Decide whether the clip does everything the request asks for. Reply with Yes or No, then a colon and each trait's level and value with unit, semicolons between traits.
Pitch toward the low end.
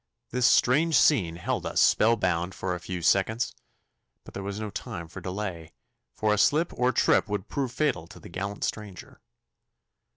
Yes: low, 100 Hz